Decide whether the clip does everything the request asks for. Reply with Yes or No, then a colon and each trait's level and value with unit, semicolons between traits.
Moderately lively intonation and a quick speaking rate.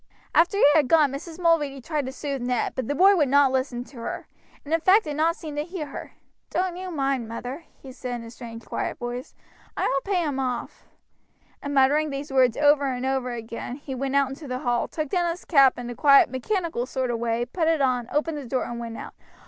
Yes: average, 3.7 semitones; fast, 235 wpm